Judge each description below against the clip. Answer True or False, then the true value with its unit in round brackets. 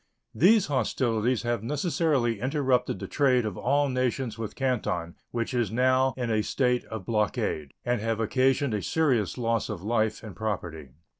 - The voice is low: True (120 Hz)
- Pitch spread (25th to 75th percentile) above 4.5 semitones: False (3.3 semitones)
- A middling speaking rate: True (160 wpm)